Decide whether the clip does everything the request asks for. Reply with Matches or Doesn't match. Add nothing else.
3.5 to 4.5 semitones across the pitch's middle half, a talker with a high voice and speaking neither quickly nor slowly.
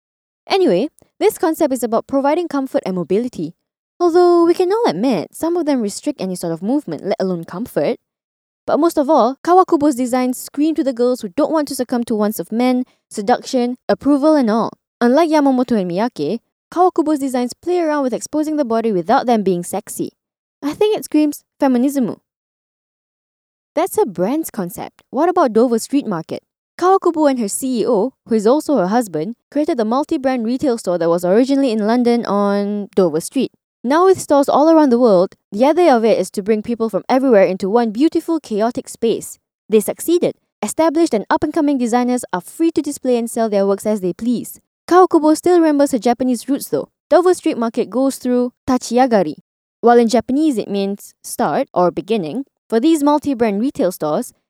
Doesn't match